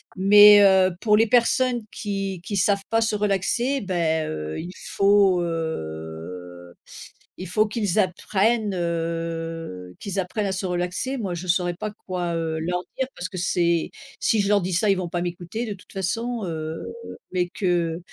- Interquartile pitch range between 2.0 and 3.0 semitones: No, average, 3.5 semitones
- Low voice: No, medium, 185 Hz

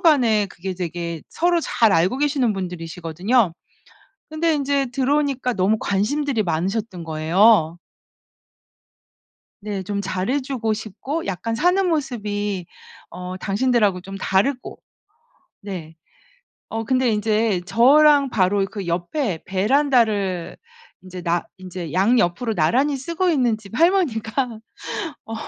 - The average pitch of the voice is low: No, high, 215 Hz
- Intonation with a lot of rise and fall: Yes, wide, 6.2 semitones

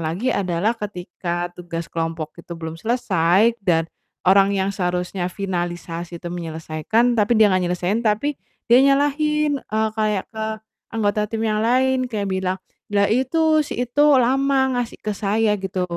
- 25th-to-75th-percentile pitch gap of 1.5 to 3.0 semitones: No, average, 5.2 semitones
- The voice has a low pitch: No, high, 205 Hz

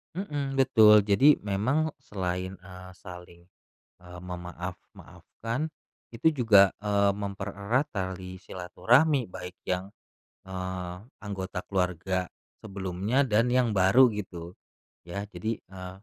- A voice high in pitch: No, low, 100 Hz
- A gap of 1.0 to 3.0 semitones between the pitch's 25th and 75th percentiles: No, average, 3.8 semitones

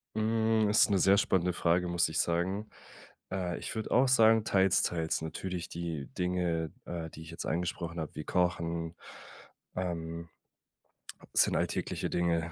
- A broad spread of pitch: No, narrow, 2.5 semitones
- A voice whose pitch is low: Yes, very low, 85 Hz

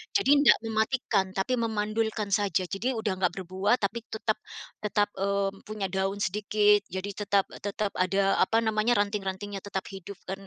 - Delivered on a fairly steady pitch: Yes, narrow, 1.7 semitones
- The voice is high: Yes, high, 205 Hz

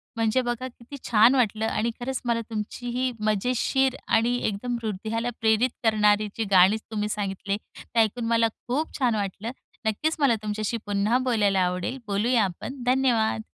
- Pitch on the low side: No, high, 225 Hz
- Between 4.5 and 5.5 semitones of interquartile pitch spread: No, average, 2.8 semitones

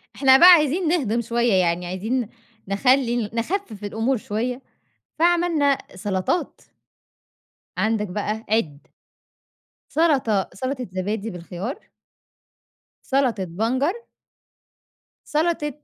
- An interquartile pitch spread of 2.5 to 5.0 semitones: No, wide, 5.5 semitones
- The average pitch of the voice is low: No, high, 235 Hz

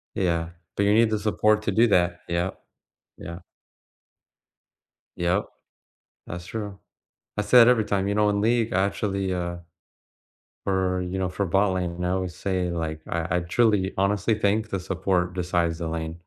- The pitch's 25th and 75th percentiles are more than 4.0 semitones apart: No, average, 2.9 semitones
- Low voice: Yes, very low, 95 Hz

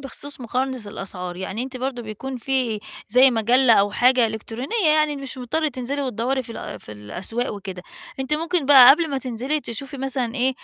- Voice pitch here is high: Yes, very high, 255 Hz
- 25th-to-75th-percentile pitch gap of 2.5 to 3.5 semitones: Yes, average, 3.2 semitones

